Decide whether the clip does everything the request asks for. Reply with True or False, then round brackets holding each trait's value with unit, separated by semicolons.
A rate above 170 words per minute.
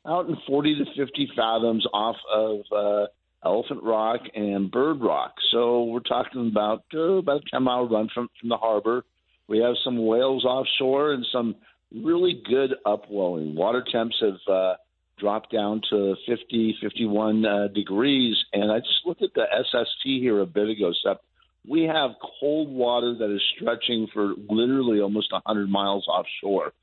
False (165 wpm)